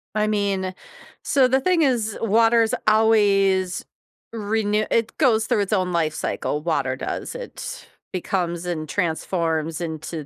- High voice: Yes, high, 200 Hz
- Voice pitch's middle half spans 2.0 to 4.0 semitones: No, average, 4.7 semitones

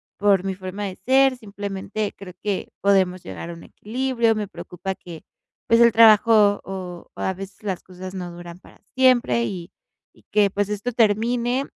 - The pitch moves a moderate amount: Yes, average, 3.3 semitones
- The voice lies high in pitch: Yes, high, 200 Hz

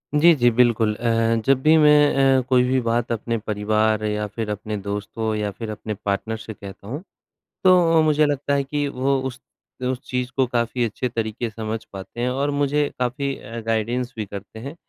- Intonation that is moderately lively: Yes, average, 3.9 semitones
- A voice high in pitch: No, low, 120 Hz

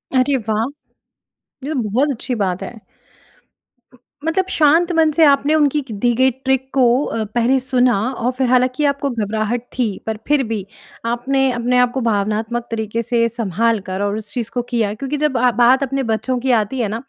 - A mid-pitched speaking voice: No, high, 245 Hz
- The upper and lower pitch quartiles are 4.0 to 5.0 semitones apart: No, average, 3.2 semitones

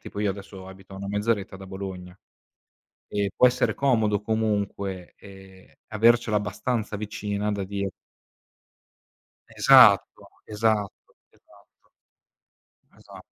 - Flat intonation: Yes, narrow, 1.8 semitones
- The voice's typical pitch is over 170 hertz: No, low, 100 Hz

